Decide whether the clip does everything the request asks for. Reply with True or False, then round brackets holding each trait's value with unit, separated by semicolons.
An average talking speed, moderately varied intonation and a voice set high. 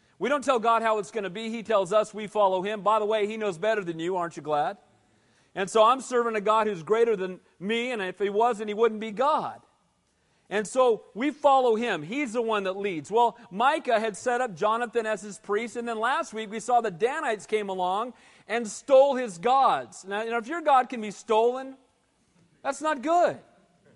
False (225 wpm; 3.1 semitones; 220 Hz)